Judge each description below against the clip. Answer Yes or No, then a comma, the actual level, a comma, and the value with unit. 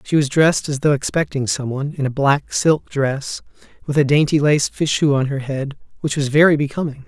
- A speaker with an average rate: No, fast, 210 wpm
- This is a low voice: No, medium, 145 Hz